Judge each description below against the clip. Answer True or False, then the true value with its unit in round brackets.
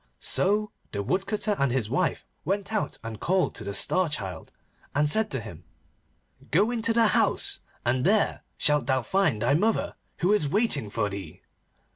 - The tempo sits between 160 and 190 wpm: True (170 wpm)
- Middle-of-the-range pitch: True (150 Hz)